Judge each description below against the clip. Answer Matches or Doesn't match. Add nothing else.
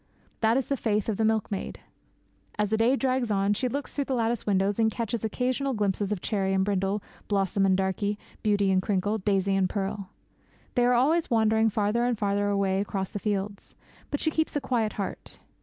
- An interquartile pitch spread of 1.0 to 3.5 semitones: Matches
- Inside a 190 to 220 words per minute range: Matches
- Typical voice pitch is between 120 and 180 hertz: Doesn't match